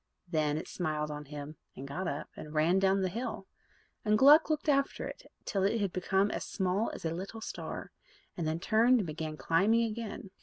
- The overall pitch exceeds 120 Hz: Yes, high, 190 Hz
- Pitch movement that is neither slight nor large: No, wide, 5.8 semitones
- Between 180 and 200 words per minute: Yes, average, 195 wpm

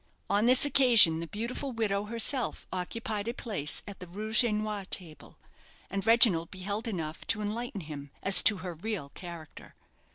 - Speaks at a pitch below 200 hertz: No, high, 205 Hz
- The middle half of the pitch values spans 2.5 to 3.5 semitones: No, average, 4.3 semitones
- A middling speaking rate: Yes, average, 165 wpm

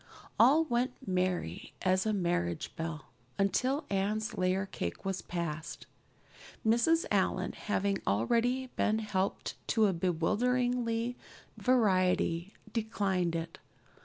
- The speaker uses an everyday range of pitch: Yes, average, 4.9 semitones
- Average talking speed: No, slow, 105 wpm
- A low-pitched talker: No, high, 195 Hz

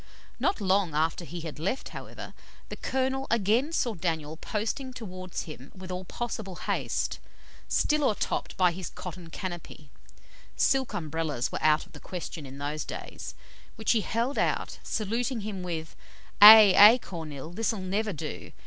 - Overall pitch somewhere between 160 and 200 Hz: Yes, medium, 185 Hz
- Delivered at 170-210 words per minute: No, average, 160 wpm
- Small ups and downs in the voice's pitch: No, wide, 5.6 semitones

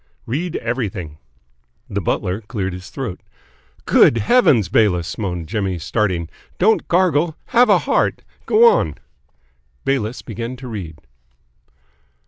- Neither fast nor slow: No, slow, 115 wpm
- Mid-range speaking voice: No, low, 110 Hz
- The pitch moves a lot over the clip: Yes, wide, 7.7 semitones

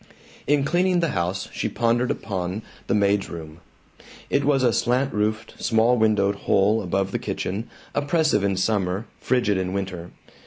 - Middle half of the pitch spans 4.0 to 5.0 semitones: Yes, average, 4.5 semitones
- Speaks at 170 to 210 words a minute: No, average, 155 wpm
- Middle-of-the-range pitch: No, low, 105 Hz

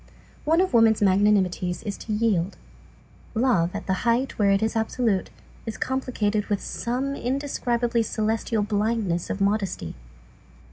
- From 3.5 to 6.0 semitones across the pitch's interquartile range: No, average, 3.1 semitones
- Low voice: No, high, 220 Hz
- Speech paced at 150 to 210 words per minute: No, slow, 135 wpm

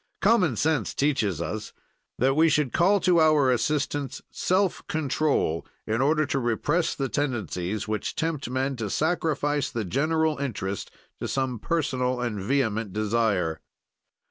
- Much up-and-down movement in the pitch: Yes, wide, 5.8 semitones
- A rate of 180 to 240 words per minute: No, average, 140 wpm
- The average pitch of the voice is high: No, low, 135 Hz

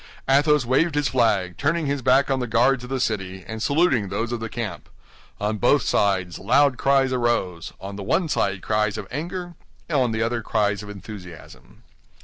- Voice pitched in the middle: No, low, 120 Hz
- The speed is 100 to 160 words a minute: No, average, 180 wpm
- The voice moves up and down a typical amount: Yes, average, 4.9 semitones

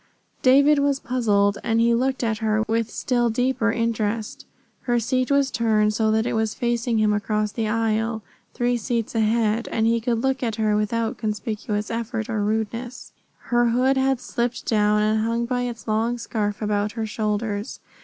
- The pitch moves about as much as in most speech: No, narrow, 2.0 semitones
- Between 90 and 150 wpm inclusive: No, average, 175 wpm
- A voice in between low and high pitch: No, high, 225 Hz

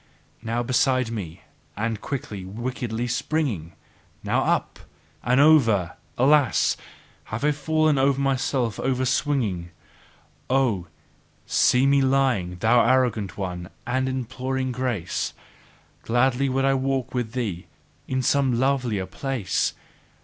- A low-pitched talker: Yes, low, 125 Hz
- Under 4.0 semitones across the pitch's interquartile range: Yes, average, 3.6 semitones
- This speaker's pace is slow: Yes, slow, 110 wpm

